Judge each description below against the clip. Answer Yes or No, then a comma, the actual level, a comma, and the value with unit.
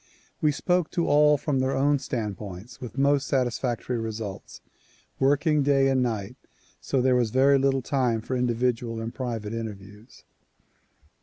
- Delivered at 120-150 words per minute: Yes, average, 145 wpm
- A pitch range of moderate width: Yes, average, 3.5 semitones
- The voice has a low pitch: Yes, low, 125 Hz